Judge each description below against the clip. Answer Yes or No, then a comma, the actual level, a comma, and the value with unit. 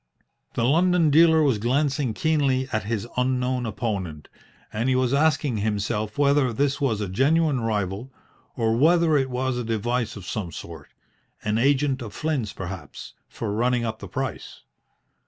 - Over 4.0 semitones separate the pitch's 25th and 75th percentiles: Yes, average, 4.6 semitones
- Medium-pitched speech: No, low, 125 Hz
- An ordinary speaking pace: Yes, average, 155 wpm